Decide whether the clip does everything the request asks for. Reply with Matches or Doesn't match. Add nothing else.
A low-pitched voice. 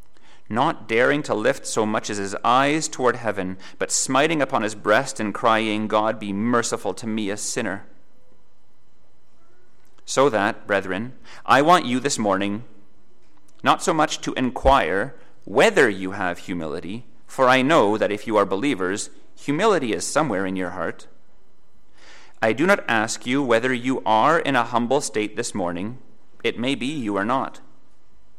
Matches